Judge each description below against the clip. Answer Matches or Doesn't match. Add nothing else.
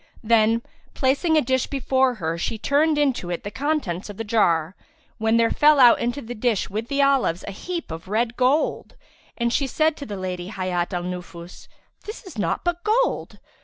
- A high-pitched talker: Matches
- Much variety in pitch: Matches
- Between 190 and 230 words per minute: Matches